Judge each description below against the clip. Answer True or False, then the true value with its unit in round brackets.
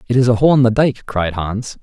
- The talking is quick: True (295 wpm)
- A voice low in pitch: True (115 Hz)